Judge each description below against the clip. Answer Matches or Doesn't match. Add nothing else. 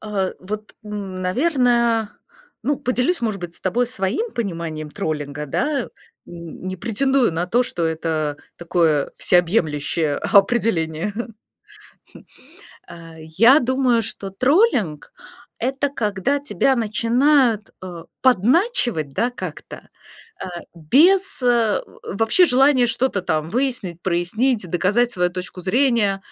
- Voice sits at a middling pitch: Doesn't match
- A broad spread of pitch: Matches